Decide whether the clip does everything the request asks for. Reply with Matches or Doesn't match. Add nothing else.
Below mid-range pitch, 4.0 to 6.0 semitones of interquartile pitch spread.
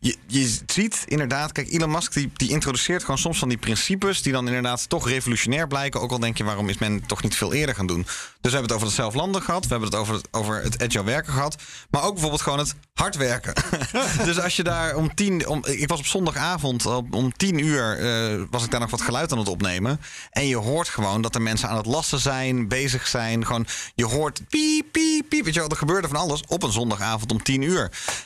Matches